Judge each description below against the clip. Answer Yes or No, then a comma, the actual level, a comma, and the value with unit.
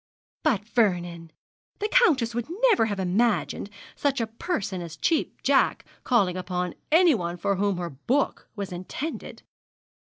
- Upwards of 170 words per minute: No, average, 140 wpm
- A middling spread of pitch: No, wide, 6.6 semitones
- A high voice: Yes, high, 205 Hz